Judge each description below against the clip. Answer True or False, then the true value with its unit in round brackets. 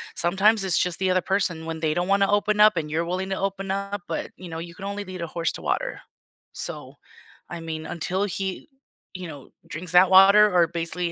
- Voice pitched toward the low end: False (185 Hz)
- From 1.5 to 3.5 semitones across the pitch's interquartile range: True (2.7 semitones)